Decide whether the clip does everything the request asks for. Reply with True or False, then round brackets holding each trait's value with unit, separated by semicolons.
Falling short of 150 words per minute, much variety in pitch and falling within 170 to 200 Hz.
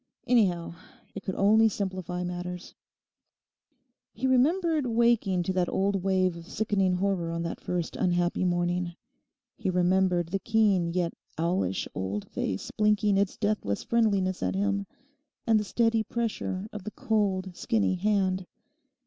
False (140 wpm; 3.0 semitones; 190 Hz)